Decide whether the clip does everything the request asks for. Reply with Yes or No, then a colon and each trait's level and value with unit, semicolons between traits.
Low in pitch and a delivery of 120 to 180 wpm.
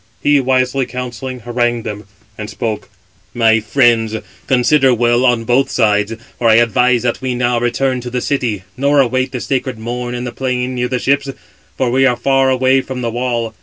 No: low, 125 Hz; average, 190 wpm